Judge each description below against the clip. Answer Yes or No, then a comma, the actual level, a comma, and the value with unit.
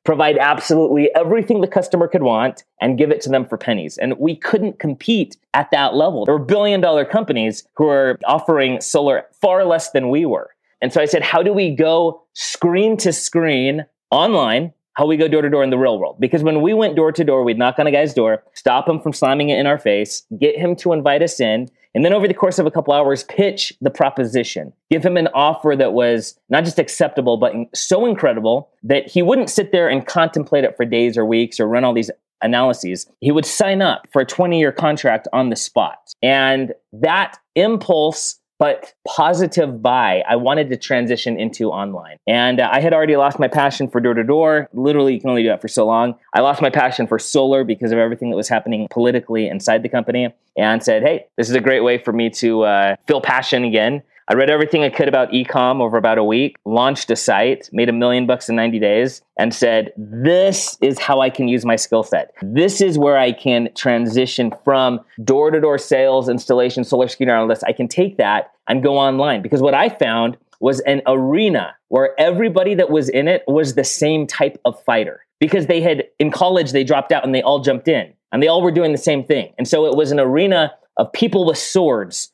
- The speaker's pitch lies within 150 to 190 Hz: No, medium, 140 Hz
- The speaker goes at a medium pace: No, fast, 220 wpm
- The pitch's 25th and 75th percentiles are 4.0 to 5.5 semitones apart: Yes, average, 4.8 semitones